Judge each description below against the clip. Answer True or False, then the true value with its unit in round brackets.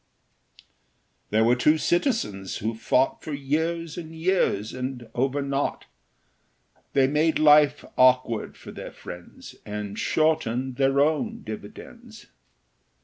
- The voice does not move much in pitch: False (5.1 semitones)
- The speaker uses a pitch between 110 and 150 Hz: True (140 Hz)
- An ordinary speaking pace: False (115 wpm)